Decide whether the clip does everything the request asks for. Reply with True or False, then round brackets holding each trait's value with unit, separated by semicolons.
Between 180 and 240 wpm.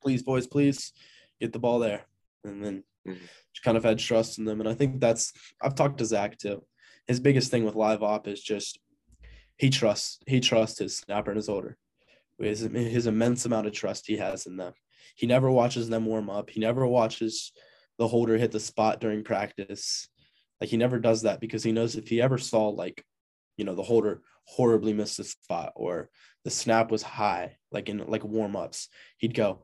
True (200 wpm)